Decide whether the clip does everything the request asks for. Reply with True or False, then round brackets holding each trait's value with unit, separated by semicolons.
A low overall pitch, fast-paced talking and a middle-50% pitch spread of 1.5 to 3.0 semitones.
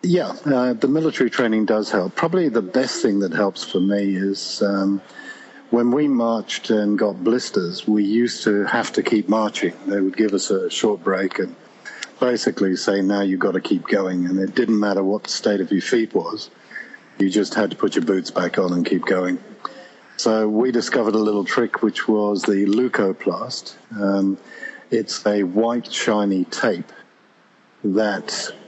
False (105 Hz; 180 wpm; 2.5 semitones)